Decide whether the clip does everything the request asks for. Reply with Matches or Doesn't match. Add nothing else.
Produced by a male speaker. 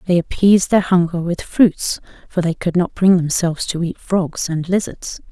Doesn't match